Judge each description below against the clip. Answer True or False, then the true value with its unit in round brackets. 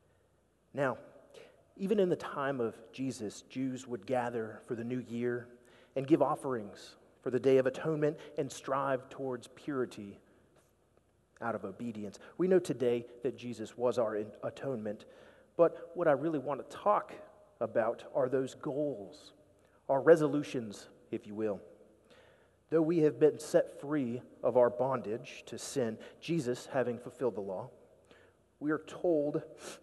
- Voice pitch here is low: True (130 Hz)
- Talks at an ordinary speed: True (145 wpm)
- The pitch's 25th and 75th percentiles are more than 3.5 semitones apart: True (4.0 semitones)